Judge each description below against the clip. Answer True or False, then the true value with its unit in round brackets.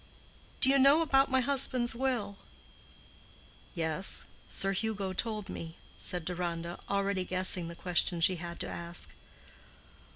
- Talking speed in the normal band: False (130 wpm)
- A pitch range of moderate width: False (5.7 semitones)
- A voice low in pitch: False (190 Hz)